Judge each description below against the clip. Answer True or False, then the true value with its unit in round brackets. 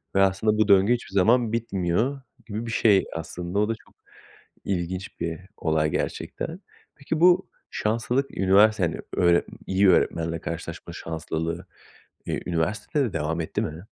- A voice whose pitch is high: False (95 Hz)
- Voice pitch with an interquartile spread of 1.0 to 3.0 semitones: False (4.8 semitones)